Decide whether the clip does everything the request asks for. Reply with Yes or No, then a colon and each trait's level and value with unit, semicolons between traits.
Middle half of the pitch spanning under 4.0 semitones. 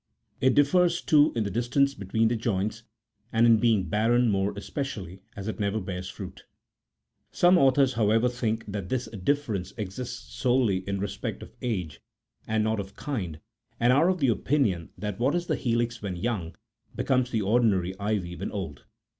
No: average, 4.3 semitones